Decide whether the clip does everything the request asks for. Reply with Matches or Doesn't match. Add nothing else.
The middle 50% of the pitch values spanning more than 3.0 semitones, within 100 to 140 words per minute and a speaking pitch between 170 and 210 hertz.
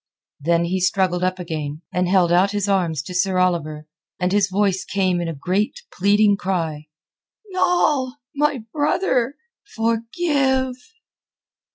Matches